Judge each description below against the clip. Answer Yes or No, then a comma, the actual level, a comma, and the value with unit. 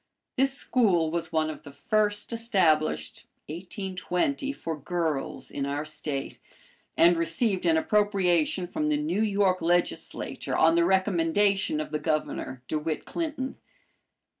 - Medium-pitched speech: Yes, medium, 175 Hz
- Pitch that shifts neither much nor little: Yes, average, 4.7 semitones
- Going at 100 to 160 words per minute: Yes, slow, 135 wpm